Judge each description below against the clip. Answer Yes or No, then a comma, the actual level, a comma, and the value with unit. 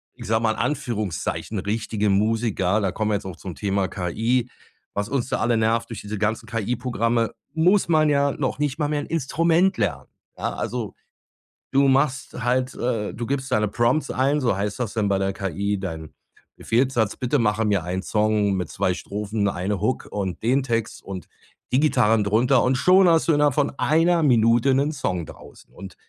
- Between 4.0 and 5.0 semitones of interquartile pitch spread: Yes, average, 4.7 semitones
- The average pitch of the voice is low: Yes, low, 115 Hz